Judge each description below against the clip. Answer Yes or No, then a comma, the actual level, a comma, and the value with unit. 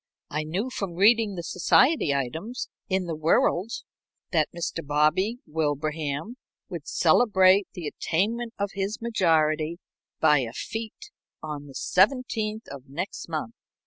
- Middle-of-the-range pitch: Yes, medium, 175 Hz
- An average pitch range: No, wide, 5.9 semitones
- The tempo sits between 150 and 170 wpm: No, slow, 135 wpm